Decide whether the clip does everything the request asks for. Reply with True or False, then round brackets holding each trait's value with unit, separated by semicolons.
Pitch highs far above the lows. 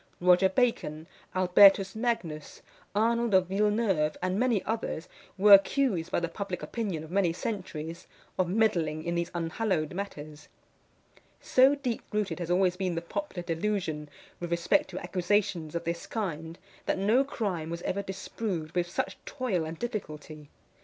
False (4.0 semitones)